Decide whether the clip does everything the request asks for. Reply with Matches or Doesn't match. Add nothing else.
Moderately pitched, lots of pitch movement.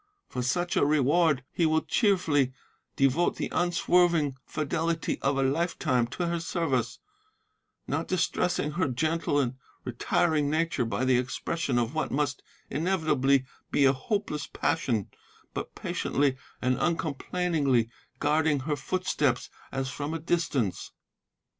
Doesn't match